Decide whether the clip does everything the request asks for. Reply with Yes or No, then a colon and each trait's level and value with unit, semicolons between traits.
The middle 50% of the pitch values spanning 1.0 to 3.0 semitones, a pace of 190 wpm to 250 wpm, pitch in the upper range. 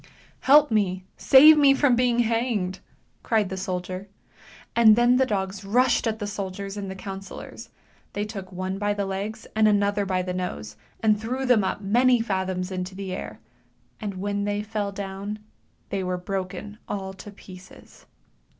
No: average, 2.7 semitones; average, 175 wpm; high, 200 Hz